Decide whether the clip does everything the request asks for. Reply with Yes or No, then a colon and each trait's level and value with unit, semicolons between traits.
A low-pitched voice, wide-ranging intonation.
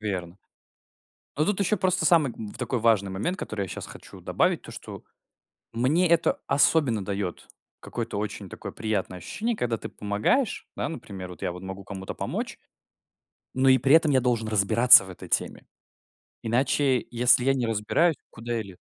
Yes: low, 115 Hz; wide, 5.7 semitones